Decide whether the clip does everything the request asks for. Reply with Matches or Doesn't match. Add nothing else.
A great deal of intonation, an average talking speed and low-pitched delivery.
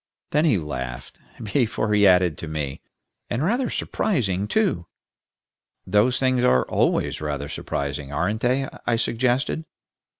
Doesn't match